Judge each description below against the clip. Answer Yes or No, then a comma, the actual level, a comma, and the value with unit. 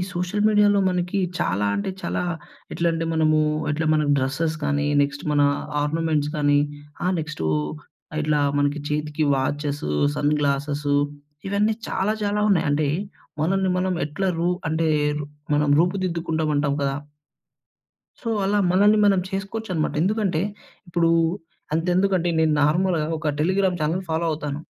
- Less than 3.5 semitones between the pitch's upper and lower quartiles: No, average, 4.1 semitones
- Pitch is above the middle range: No, medium, 160 Hz